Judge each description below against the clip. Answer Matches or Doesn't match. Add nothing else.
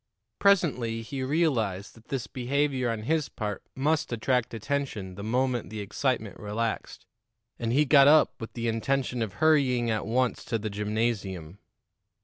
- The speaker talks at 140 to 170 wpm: Matches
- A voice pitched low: Matches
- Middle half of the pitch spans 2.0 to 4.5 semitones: Matches